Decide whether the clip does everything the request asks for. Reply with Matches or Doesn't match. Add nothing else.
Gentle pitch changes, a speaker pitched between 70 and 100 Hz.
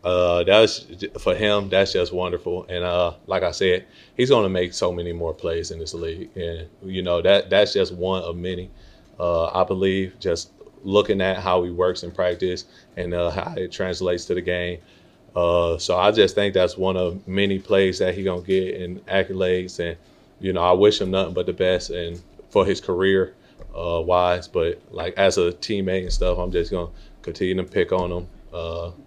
Matches